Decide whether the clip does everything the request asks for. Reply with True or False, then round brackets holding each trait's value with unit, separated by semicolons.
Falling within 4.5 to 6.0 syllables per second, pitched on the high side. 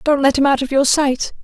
True (5.5 syllables/s; 275 Hz)